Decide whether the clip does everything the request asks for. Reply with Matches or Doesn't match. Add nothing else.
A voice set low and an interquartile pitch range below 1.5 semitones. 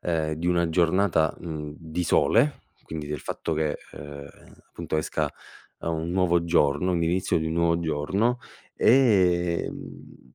Doesn't match